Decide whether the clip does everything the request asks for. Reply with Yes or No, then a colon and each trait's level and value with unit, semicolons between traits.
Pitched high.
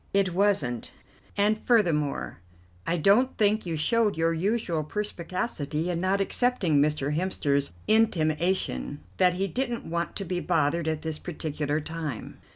No: medium, 170 Hz